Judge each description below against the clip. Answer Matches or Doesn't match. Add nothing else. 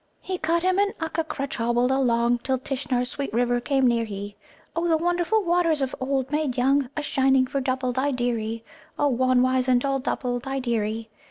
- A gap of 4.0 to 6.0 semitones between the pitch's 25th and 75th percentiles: Doesn't match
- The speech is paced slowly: Doesn't match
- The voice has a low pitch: Doesn't match